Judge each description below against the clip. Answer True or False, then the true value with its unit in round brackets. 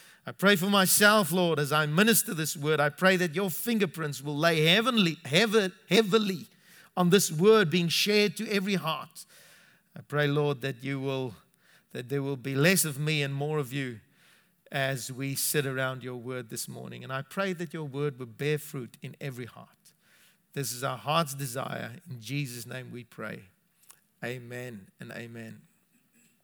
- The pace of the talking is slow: False (175 wpm)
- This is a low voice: False (150 Hz)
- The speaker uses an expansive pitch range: True (5.7 semitones)